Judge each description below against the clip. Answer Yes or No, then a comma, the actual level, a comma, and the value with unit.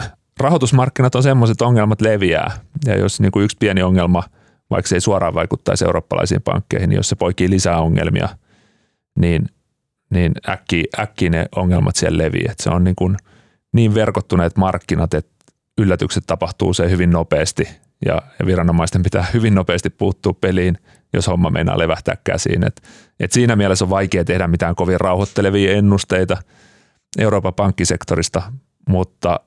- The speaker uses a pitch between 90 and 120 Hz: Yes, very low, 95 Hz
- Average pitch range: Yes, average, 3.1 semitones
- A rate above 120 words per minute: Yes, average, 145 wpm